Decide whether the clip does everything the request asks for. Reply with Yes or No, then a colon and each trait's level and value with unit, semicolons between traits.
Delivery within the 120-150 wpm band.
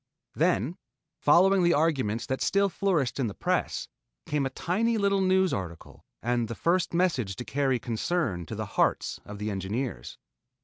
No: average, 165 wpm